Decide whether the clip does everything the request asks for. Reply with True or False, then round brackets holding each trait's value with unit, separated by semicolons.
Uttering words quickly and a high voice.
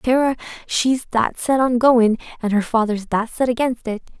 False (185 wpm; 240 Hz)